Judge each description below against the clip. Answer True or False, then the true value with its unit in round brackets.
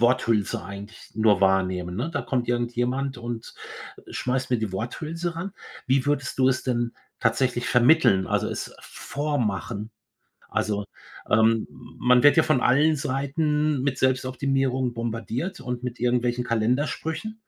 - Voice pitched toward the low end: True (125 Hz)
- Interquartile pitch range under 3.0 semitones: False (3.3 semitones)